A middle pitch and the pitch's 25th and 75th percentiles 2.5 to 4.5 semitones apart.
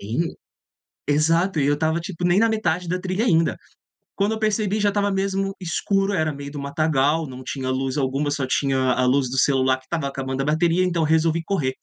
No: medium, 160 Hz; average, 5.2 semitones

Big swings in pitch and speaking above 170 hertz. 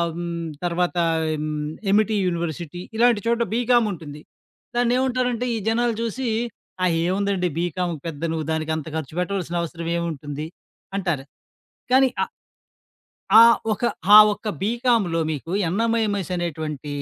Yes: wide, 5.7 semitones; medium, 180 Hz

